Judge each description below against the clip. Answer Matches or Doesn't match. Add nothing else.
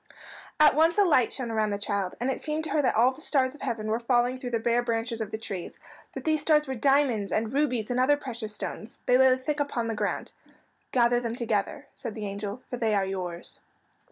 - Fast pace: Matches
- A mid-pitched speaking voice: Doesn't match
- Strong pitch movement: Doesn't match